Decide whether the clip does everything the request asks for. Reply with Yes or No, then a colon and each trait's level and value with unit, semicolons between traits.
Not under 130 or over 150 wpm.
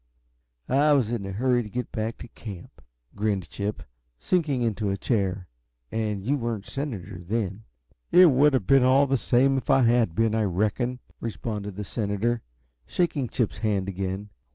No: average, 175 wpm